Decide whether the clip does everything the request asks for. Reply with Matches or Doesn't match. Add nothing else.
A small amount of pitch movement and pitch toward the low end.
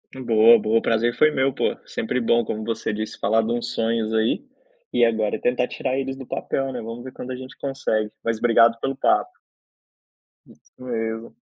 Matches